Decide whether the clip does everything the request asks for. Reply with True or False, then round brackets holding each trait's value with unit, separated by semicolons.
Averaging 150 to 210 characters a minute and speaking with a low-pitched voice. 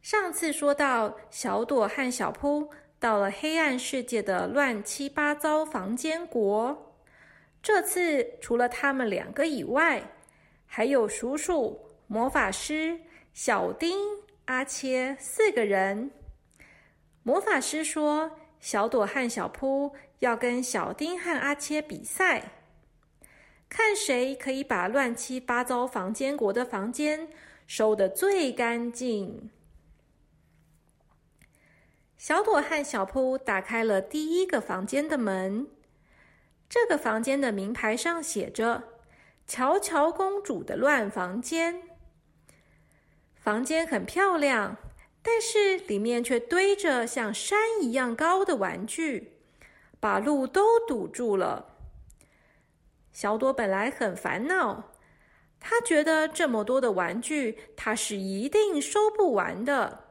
False (170 characters per minute; 265 Hz)